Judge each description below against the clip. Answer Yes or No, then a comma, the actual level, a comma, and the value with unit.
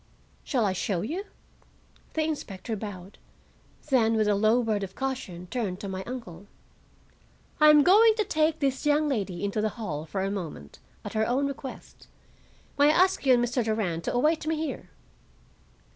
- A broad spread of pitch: Yes, wide, 6.8 semitones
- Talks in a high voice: Yes, high, 230 Hz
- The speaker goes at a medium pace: Yes, average, 175 wpm